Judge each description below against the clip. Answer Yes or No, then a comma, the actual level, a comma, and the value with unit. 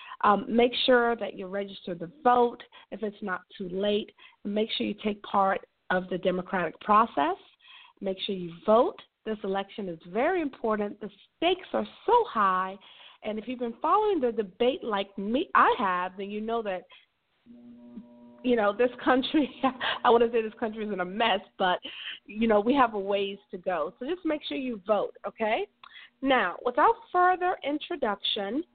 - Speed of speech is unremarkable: Yes, average, 175 wpm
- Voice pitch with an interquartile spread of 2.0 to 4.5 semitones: No, average, 5.1 semitones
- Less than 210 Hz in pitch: No, high, 225 Hz